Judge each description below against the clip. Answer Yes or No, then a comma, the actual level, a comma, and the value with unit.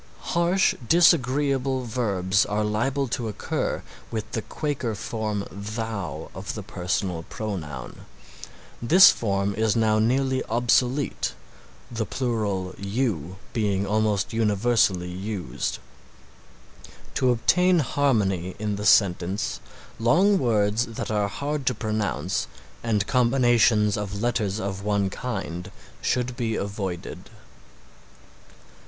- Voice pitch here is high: No, low, 110 Hz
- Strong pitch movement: No, average, 3.8 semitones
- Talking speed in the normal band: No, slow, 110 wpm